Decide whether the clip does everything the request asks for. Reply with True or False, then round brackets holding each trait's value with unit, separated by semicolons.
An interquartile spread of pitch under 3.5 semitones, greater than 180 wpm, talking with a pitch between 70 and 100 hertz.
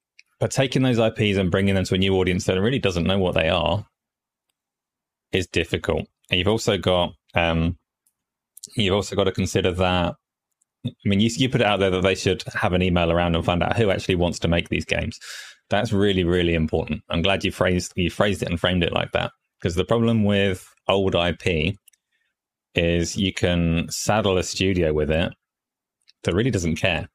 True (2.8 semitones; 200 wpm; 95 Hz)